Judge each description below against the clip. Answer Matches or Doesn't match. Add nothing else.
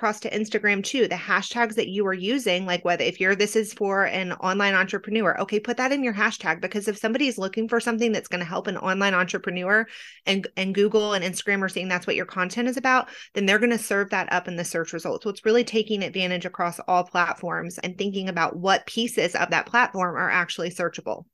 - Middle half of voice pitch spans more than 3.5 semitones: Doesn't match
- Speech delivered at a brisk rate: Matches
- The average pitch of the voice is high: Matches